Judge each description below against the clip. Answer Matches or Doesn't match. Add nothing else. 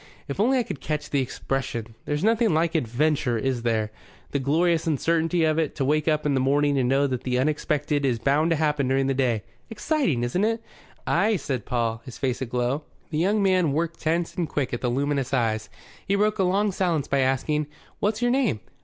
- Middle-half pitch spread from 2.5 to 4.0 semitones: Doesn't match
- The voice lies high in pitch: Doesn't match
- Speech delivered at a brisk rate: Matches